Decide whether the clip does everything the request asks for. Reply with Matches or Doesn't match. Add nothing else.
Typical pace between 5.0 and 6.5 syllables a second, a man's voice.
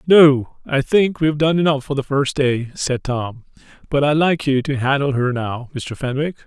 Doesn't match